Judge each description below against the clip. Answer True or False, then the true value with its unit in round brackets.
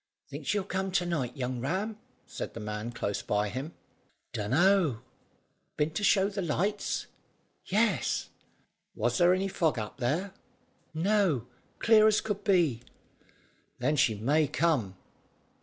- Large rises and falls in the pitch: True (8.0 semitones)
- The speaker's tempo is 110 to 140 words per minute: True (135 wpm)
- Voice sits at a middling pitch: True (160 Hz)